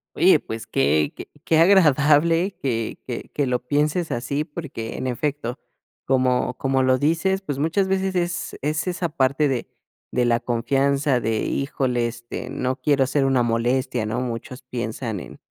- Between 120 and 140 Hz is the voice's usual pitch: Yes, low, 135 Hz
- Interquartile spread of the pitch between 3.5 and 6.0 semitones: Yes, average, 3.9 semitones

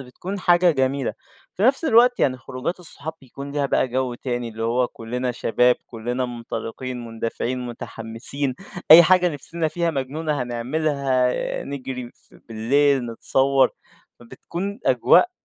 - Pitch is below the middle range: Yes, low, 130 Hz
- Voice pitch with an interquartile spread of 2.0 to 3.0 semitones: No, average, 4.2 semitones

